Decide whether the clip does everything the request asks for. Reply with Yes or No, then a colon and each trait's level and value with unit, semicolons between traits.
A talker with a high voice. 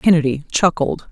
No: medium, 160 Hz